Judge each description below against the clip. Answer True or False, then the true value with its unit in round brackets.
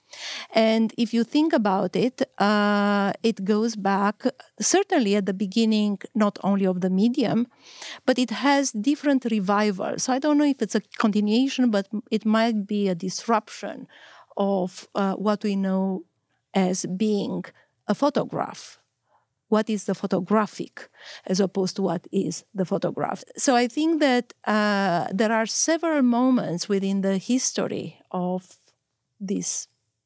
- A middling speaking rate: True (145 wpm)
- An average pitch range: True (3.6 semitones)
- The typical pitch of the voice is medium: False (210 Hz)